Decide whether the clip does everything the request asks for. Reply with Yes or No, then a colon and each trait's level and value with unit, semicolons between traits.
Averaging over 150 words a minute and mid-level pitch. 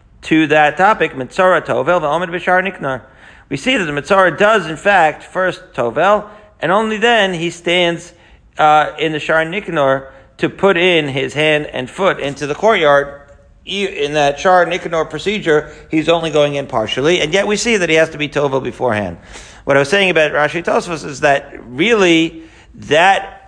Yes: average, 175 wpm; medium, 160 Hz